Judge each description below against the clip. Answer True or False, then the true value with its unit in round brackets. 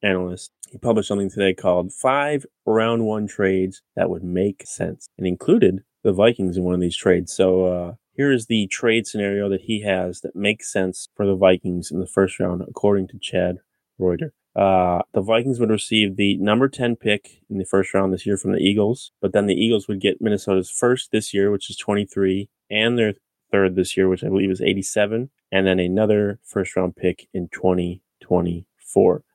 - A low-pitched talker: True (100 Hz)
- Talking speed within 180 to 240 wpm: True (195 wpm)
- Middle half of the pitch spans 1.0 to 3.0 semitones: True (2.5 semitones)